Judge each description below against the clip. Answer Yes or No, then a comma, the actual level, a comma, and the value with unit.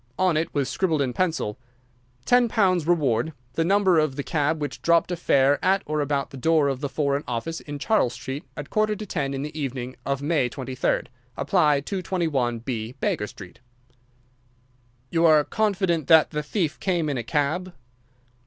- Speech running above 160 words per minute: Yes, average, 170 wpm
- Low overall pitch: No, medium, 150 Hz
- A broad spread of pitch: No, average, 4.2 semitones